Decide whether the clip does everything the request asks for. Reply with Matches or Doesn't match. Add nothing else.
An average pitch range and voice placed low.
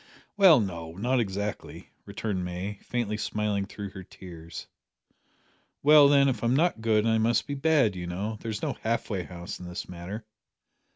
Matches